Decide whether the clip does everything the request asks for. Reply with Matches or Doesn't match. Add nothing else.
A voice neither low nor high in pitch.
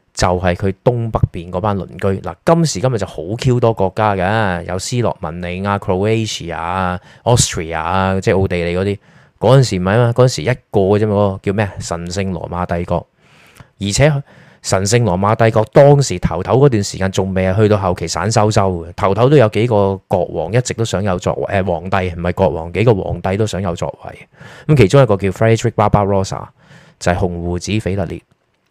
Doesn't match